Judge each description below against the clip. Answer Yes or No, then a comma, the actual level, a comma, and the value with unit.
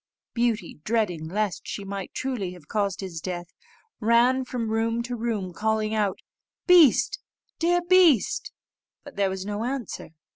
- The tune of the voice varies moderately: Yes, average, 4.1 semitones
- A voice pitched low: No, high, 220 Hz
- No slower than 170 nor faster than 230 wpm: No, average, 145 wpm